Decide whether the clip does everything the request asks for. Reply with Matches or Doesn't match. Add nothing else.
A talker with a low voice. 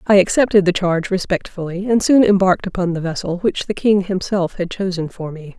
Doesn't match